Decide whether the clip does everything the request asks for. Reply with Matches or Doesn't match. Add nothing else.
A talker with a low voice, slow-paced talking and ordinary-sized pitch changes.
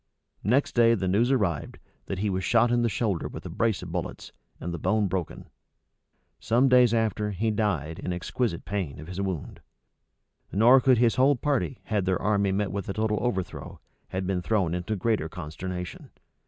Doesn't match